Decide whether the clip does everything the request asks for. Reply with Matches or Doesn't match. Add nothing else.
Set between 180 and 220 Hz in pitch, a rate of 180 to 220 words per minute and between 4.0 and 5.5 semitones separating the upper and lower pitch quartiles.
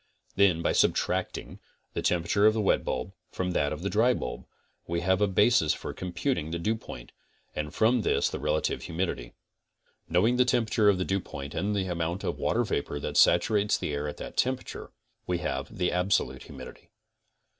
Doesn't match